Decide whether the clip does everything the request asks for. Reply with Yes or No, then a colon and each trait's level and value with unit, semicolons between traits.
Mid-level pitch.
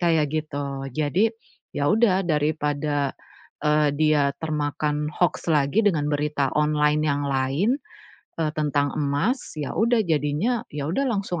Yes: medium, 150 Hz